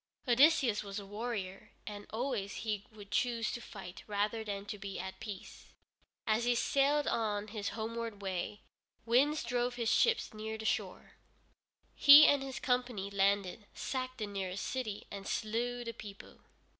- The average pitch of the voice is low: No, high, 220 Hz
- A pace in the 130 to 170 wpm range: Yes, average, 155 wpm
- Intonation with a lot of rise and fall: No, average, 3.3 semitones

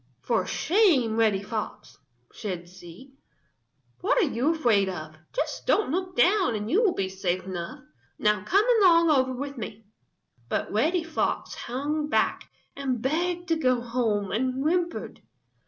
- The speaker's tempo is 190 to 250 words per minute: No, average, 150 wpm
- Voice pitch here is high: Yes, very high, 255 Hz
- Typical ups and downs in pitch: No, wide, 8.1 semitones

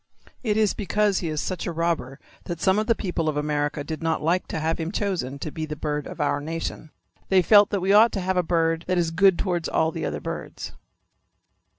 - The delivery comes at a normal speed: No, fast, 235 wpm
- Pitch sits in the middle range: Yes, medium, 170 Hz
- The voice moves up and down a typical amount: Yes, average, 3.4 semitones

